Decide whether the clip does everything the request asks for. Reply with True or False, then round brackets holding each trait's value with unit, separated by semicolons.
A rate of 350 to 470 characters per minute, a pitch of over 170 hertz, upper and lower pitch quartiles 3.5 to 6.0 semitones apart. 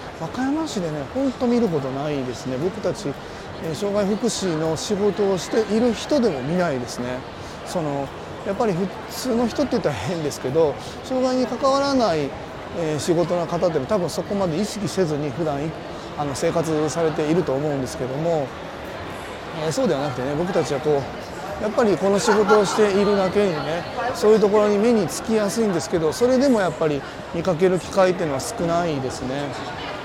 True (365 characters per minute; 185 Hz; 5.7 semitones)